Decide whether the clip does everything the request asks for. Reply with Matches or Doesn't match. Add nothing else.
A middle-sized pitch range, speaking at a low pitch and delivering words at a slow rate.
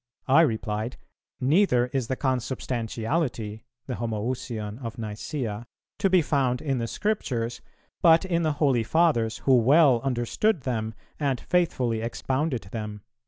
Matches